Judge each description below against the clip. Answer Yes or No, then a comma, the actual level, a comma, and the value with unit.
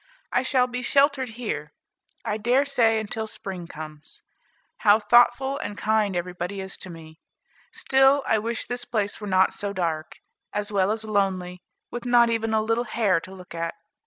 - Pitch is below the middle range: No, high, 215 Hz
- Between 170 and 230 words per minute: Yes, average, 175 wpm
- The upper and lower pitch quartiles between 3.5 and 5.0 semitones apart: Yes, average, 4.5 semitones